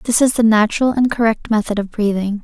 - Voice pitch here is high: Yes, high, 220 Hz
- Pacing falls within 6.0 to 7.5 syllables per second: Yes, 6.1 syllables/s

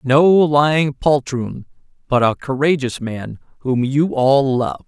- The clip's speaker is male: Yes, male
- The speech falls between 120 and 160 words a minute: Yes, slow, 135 wpm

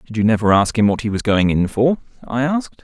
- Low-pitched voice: Yes, low, 115 Hz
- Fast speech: Yes, fast, 275 wpm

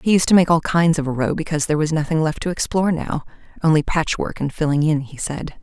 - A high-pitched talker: No, medium, 155 Hz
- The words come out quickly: Yes, fast, 255 wpm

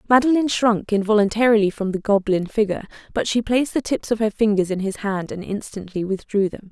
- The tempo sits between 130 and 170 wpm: No, average, 195 wpm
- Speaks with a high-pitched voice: Yes, high, 210 Hz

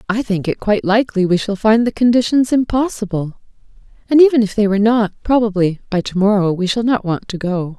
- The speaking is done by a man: No, female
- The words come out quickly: Yes, fast, 210 wpm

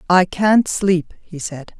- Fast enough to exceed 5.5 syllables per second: No, 3.3 syllables/s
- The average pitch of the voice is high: No, medium, 180 Hz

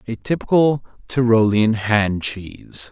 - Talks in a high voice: No, low, 115 Hz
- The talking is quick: No, slow, 105 wpm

